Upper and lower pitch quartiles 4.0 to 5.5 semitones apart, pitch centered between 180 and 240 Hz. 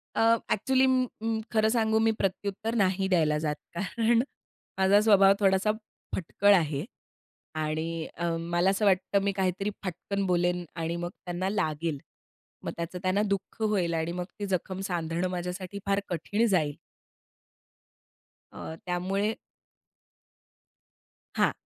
No: average, 2.9 semitones; medium, 185 Hz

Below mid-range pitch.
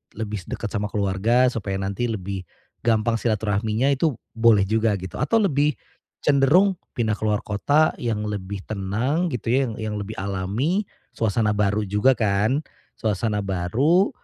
Yes: low, 110 Hz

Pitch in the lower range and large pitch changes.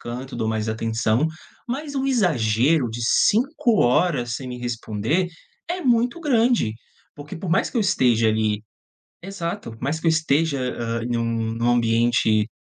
Yes: low, 125 Hz; wide, 8.2 semitones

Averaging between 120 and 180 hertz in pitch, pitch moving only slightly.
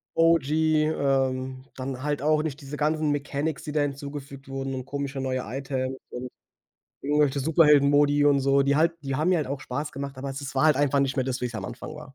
Yes: medium, 140 Hz; narrow, 1.8 semitones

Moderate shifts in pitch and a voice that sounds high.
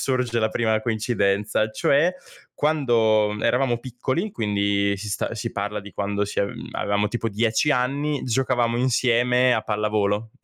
No: average, 3.2 semitones; low, 115 Hz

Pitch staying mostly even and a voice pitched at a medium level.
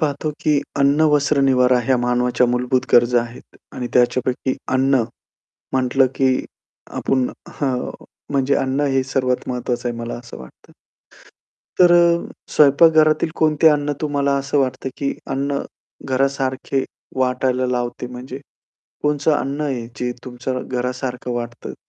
No: narrow, 2.2 semitones; low, 130 Hz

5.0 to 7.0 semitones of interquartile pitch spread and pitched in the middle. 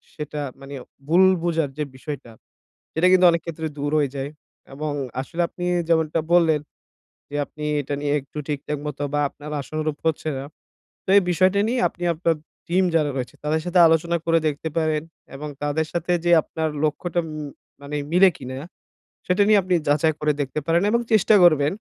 No: average, 2.8 semitones; medium, 155 Hz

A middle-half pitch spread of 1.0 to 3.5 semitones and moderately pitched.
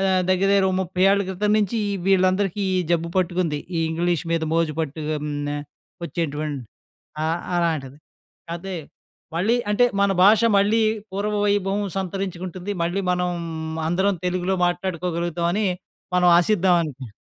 Yes: average, 2.8 semitones; medium, 180 Hz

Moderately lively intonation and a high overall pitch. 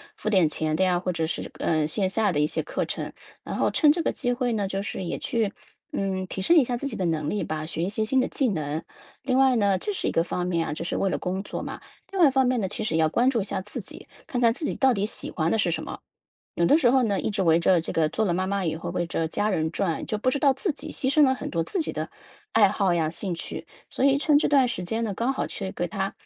No: wide, 6.7 semitones; high, 200 Hz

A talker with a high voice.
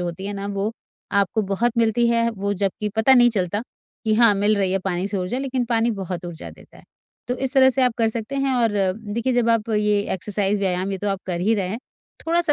Yes: high, 210 Hz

